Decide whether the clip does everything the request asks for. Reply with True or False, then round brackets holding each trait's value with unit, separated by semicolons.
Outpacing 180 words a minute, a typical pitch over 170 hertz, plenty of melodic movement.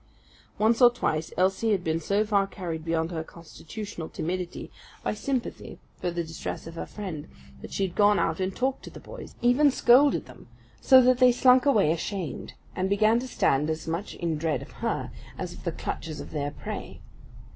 True (195 wpm; 190 Hz; 6.1 semitones)